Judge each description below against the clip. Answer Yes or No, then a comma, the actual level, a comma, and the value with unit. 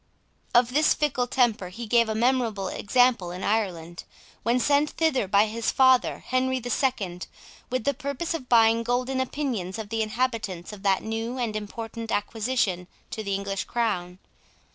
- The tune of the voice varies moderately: Yes, average, 4.0 semitones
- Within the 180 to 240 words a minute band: No, average, 165 wpm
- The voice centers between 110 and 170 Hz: No, high, 230 Hz